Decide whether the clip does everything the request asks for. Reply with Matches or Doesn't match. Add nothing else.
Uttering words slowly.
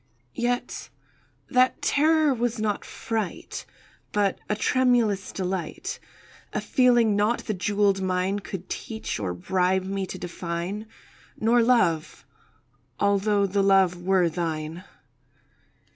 Matches